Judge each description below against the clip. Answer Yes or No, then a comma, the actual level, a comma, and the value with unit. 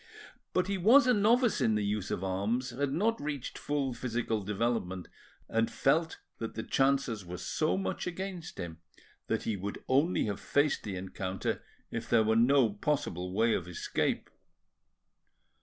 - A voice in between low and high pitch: No, low, 115 Hz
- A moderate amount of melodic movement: No, wide, 6.7 semitones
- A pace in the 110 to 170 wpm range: Yes, average, 160 wpm